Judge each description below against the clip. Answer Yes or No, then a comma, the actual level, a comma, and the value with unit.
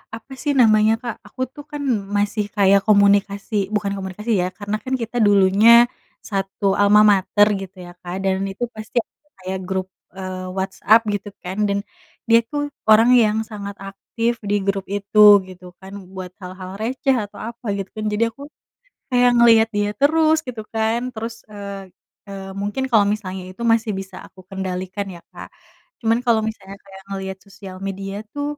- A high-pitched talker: Yes, high, 205 Hz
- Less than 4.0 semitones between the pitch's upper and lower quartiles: Yes, narrow, 2.6 semitones